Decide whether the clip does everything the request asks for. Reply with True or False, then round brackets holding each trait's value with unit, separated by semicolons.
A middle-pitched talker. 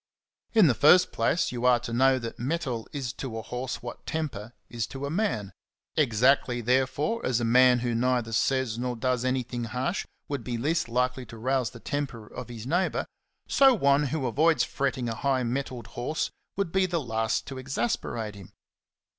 False (125 Hz)